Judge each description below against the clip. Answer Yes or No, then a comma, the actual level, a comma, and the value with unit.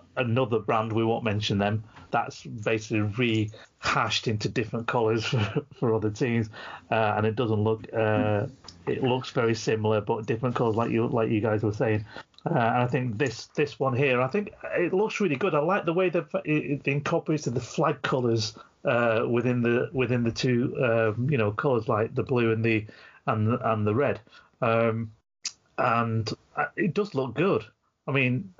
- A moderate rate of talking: Yes, average, 185 wpm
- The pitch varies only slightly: No, average, 3.7 semitones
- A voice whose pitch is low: Yes, low, 115 Hz